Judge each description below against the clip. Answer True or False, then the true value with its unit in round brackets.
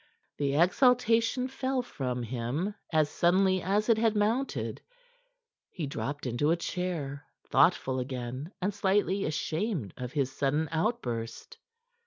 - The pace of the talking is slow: True (125 wpm)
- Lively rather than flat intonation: True (7.4 semitones)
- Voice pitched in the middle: True (165 Hz)